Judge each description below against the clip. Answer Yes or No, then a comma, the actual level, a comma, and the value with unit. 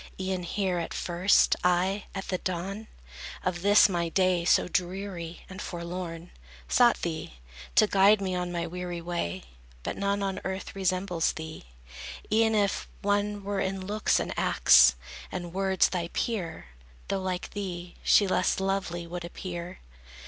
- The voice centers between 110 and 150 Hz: No, medium, 185 Hz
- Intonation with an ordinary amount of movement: No, narrow, 2.1 semitones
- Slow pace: No, average, 150 wpm